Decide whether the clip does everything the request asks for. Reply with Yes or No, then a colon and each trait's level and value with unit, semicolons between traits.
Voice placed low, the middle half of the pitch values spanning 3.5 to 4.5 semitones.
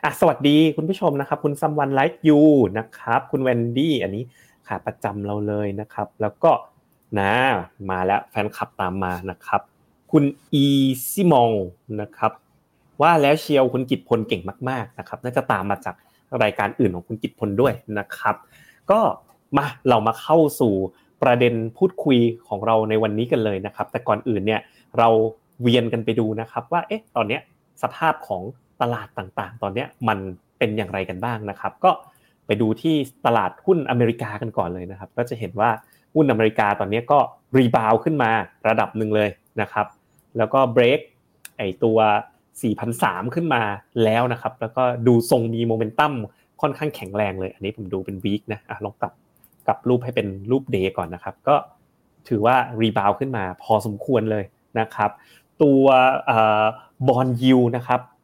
Yes: low, 115 Hz; average, 3.8 semitones